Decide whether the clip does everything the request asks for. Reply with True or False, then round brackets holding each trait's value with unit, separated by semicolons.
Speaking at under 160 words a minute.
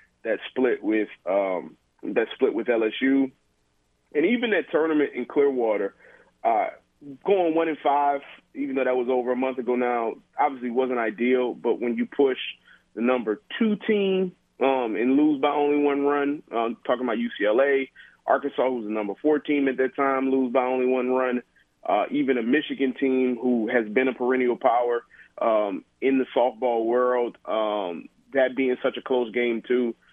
False (175 wpm)